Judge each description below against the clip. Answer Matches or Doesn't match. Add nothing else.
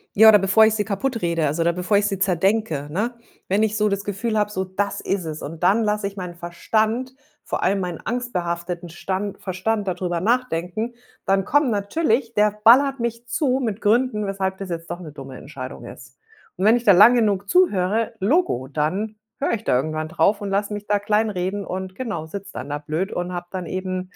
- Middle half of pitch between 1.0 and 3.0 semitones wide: Doesn't match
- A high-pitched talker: Matches